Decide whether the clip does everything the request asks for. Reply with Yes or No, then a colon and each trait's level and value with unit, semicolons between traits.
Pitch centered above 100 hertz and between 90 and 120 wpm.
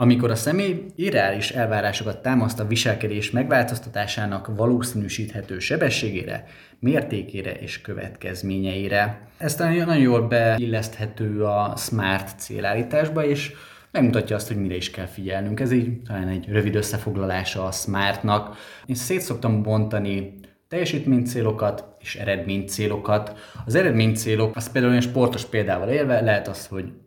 No: low, 110 Hz; average, 130 wpm